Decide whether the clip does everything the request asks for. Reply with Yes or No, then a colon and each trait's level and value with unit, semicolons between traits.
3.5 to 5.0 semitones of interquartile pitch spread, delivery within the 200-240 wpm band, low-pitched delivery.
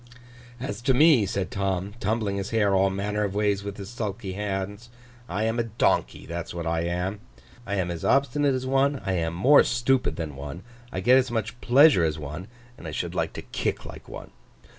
Yes: average, 4.5 semitones; fast, 205 wpm; low, 100 Hz